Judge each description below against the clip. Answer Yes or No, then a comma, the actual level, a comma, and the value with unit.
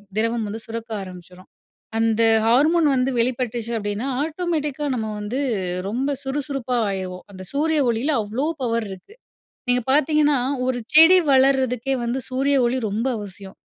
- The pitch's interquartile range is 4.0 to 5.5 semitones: Yes, average, 4.3 semitones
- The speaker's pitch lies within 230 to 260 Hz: Yes, very high, 250 Hz